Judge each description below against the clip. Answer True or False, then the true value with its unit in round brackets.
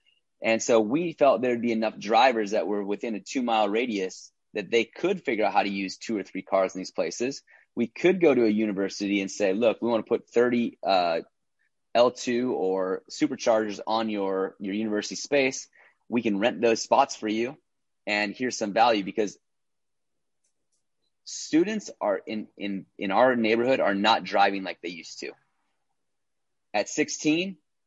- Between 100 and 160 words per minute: False (170 wpm)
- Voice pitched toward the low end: True (115 Hz)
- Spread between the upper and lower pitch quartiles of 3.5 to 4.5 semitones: True (3.9 semitones)